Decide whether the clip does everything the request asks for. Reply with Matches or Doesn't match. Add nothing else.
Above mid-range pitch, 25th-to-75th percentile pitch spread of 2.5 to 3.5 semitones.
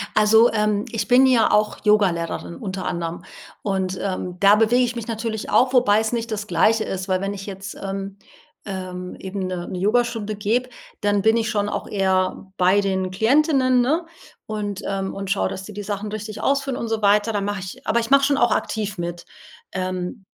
Matches